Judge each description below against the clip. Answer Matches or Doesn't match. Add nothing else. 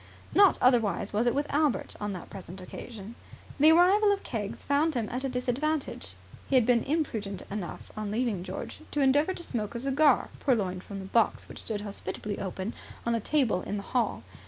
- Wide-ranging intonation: Matches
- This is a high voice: Matches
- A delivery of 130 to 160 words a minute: Doesn't match